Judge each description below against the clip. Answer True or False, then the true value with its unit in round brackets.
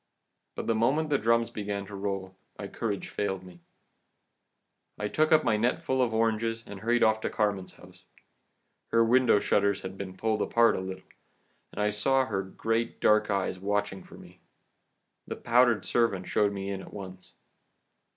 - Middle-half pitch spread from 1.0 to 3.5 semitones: True (2.9 semitones)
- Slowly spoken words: False (175 wpm)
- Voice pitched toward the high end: False (105 Hz)